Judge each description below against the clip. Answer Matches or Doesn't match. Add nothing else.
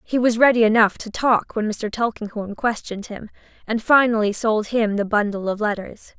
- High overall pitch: Matches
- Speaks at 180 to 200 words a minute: Matches